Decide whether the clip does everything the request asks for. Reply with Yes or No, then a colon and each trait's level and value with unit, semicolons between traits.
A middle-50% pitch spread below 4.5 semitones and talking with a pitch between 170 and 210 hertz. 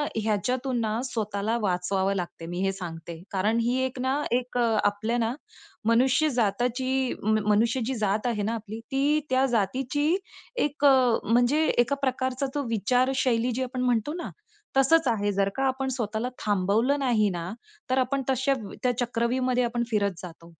No: average, 3.8 semitones; high, 240 Hz